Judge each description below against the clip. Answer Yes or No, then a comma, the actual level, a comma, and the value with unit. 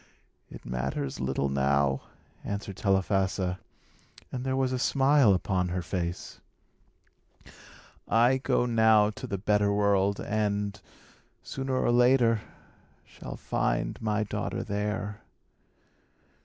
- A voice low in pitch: Yes, low, 105 Hz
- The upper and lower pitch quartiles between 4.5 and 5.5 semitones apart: No, average, 3.9 semitones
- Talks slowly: Yes, slow, 110 wpm